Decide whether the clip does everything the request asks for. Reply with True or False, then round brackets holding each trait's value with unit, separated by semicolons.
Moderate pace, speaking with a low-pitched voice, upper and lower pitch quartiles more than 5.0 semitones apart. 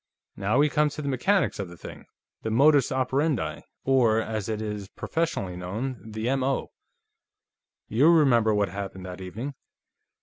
True (155 wpm; 115 Hz; 5.6 semitones)